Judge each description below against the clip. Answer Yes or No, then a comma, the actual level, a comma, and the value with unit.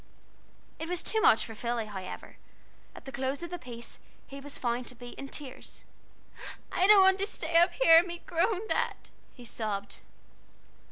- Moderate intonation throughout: No, wide, 6.7 semitones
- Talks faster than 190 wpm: Yes, average, 200 wpm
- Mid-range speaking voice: No, very high, 275 Hz